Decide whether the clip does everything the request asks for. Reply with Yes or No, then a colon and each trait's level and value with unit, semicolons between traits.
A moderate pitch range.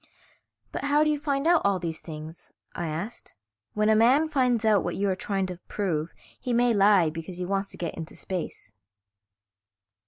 No: wide, 6.0 semitones